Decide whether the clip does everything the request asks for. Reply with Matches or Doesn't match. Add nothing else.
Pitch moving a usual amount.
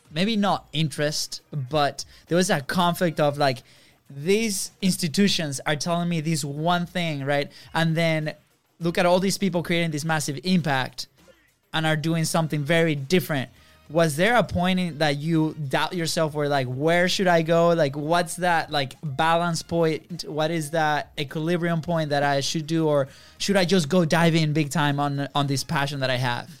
Matches